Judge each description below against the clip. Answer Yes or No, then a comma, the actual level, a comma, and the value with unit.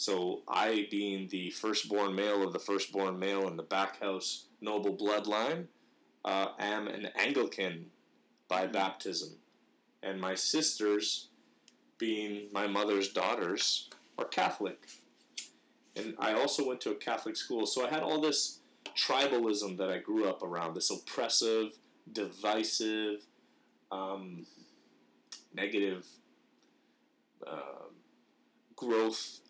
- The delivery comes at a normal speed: No, slow, 115 wpm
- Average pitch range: No, narrow, 2.0 semitones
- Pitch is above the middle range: No, low, 105 Hz